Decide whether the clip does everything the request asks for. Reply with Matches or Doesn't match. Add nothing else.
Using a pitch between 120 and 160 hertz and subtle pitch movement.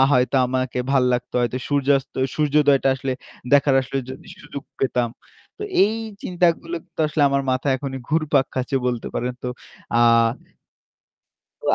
Matches